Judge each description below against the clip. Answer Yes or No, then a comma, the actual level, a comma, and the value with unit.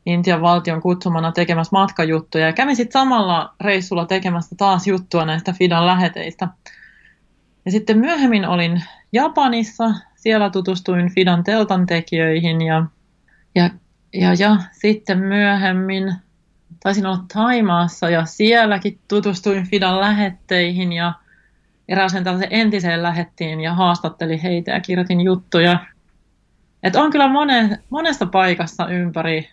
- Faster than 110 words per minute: Yes, average, 120 wpm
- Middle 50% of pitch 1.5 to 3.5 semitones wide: Yes, average, 2.9 semitones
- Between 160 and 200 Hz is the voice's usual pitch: Yes, medium, 185 Hz